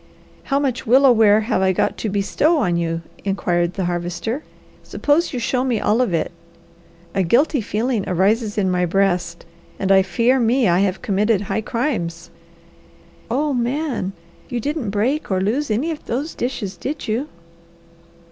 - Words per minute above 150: Yes, average, 165 wpm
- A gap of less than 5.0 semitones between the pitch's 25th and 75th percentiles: No, wide, 5.5 semitones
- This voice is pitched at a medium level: No, high, 215 Hz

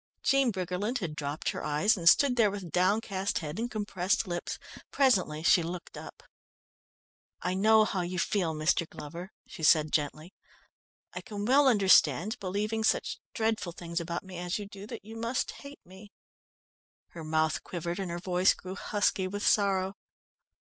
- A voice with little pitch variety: No, average, 3.8 semitones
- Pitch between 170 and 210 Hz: Yes, high, 190 Hz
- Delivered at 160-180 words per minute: Yes, average, 165 wpm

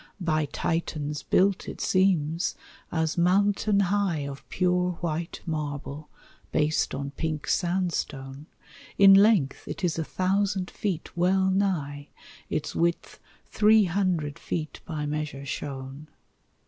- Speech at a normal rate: No, slow, 120 wpm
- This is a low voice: No, medium, 170 Hz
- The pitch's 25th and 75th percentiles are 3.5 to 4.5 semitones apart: Yes, average, 4.2 semitones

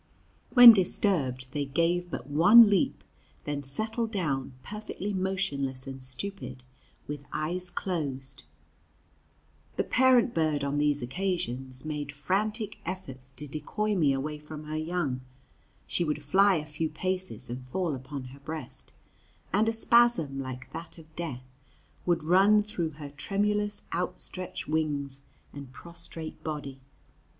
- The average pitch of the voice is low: No, medium, 155 Hz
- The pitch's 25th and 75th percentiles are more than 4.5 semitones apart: Yes, average, 5.3 semitones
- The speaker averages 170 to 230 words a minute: No, slow, 135 wpm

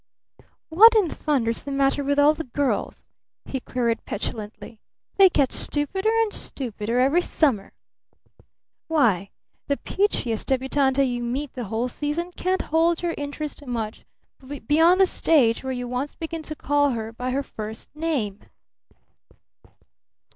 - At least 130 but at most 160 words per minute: Yes, average, 140 wpm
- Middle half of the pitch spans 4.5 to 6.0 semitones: Yes, average, 4.8 semitones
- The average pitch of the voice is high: Yes, very high, 275 Hz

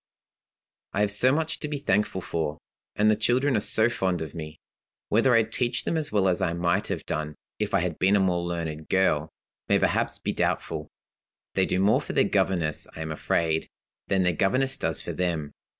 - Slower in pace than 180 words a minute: No, fast, 205 wpm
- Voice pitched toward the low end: Yes, very low, 95 Hz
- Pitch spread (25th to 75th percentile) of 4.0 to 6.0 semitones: Yes, average, 4.9 semitones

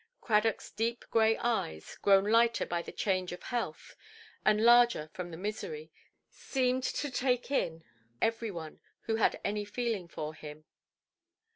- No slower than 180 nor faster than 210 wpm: No, average, 145 wpm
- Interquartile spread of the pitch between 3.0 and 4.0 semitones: No, average, 5.0 semitones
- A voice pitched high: Yes, high, 220 Hz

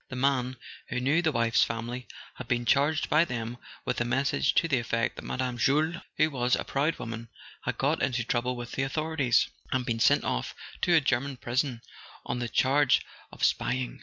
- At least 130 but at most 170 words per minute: No, average, 200 wpm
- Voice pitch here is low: Yes, low, 125 Hz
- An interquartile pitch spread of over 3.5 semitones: No, average, 2.7 semitones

